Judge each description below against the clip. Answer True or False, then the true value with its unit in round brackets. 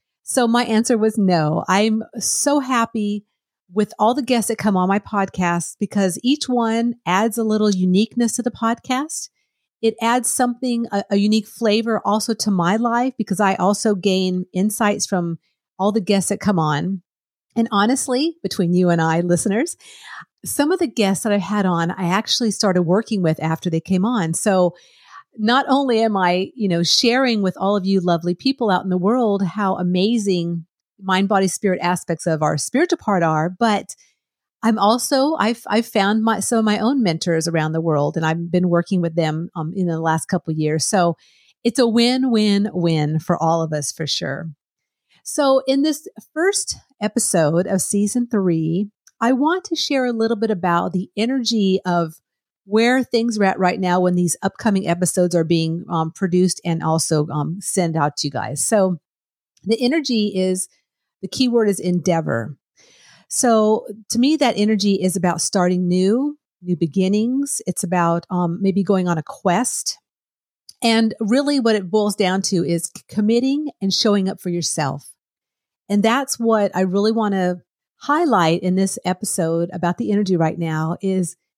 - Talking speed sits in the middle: True (180 wpm)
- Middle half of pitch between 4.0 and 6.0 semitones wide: True (4.4 semitones)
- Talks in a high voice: True (200 Hz)